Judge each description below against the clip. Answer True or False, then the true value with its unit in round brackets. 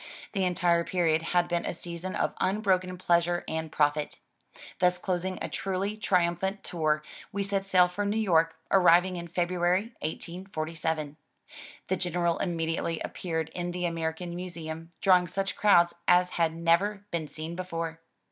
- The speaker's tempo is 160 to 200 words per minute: False (145 wpm)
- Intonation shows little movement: True (2.0 semitones)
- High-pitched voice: False (175 Hz)